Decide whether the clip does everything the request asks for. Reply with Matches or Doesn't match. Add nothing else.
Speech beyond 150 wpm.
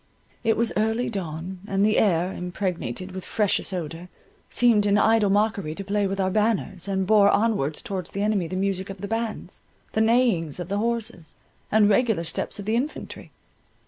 Matches